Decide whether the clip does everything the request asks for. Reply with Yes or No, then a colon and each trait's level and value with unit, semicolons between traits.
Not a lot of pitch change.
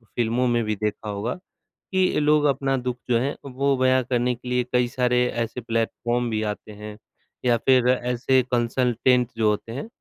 Yes: narrow, 1.8 semitones